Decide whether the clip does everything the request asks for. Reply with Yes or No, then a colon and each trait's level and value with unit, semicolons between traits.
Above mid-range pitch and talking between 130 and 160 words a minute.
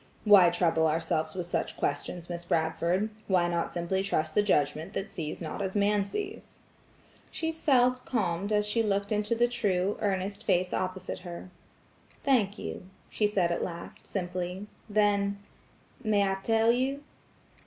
Yes: high, 195 Hz; average, 155 wpm